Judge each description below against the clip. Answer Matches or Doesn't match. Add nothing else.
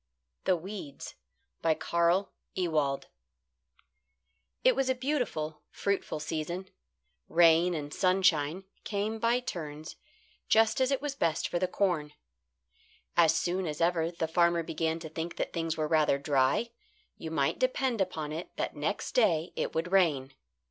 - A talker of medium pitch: Matches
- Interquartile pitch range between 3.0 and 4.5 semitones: Matches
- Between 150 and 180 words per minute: Doesn't match